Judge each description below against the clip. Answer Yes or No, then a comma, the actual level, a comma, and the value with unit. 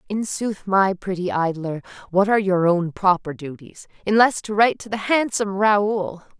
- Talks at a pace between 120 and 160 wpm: No, average, 170 wpm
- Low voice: No, high, 195 Hz